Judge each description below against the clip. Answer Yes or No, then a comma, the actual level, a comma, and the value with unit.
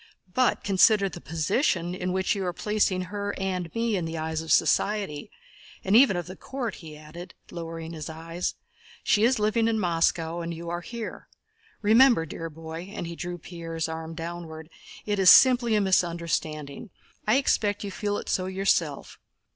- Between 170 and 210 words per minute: Yes, average, 175 wpm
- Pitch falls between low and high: Yes, medium, 180 Hz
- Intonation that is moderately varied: Yes, average, 4.0 semitones